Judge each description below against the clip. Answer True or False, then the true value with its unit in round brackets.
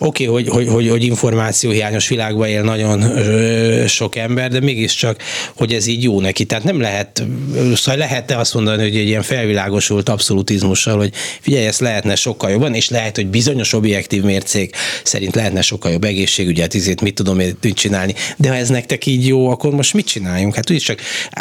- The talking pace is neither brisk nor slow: False (185 wpm)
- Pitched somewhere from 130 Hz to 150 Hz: False (110 Hz)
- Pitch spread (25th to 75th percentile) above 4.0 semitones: False (3.2 semitones)